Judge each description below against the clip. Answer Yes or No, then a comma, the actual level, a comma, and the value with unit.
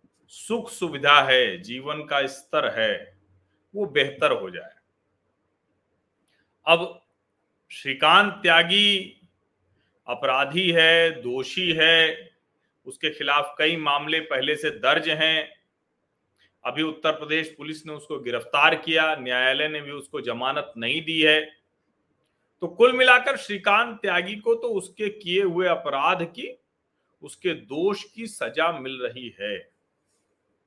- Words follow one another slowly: No, average, 120 wpm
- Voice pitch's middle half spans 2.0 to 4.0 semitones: No, wide, 5.4 semitones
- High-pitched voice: No, medium, 160 Hz